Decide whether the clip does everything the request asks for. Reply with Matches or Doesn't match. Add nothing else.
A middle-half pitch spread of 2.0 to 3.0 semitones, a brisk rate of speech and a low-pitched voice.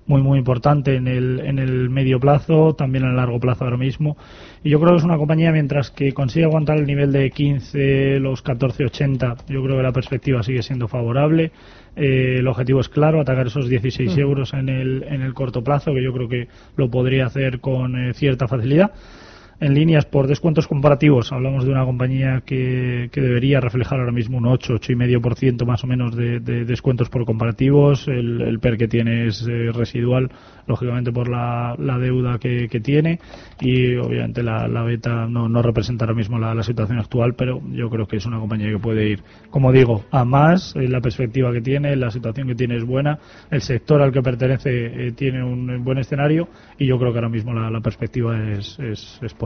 Matches